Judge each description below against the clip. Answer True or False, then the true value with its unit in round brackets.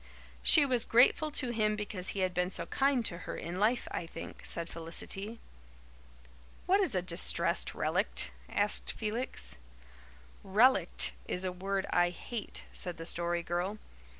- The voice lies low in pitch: False (195 Hz)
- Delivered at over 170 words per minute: False (150 wpm)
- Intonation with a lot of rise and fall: False (5.0 semitones)